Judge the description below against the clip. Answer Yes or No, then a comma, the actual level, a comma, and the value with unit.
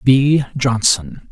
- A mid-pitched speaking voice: No, low, 130 Hz